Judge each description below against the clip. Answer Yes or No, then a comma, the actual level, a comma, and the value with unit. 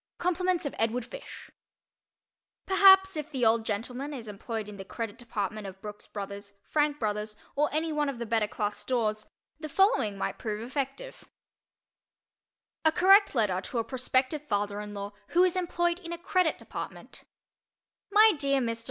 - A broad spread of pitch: Yes, wide, 7.5 semitones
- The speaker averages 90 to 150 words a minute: No, average, 170 wpm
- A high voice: Yes, very high, 250 Hz